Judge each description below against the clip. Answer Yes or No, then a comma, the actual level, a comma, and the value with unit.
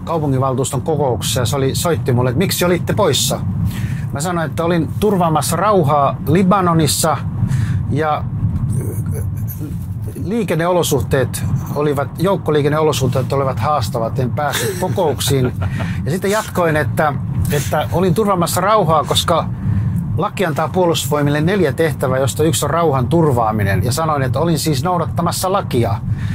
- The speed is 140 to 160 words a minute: No, average, 120 wpm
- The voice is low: No, medium, 145 Hz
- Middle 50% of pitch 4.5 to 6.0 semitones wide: Yes, average, 5.0 semitones